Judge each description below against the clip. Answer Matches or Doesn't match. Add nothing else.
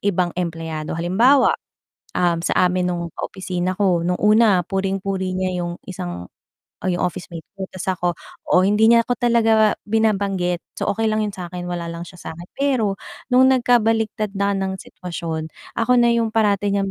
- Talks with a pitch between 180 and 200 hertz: Matches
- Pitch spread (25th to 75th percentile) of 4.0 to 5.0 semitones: Doesn't match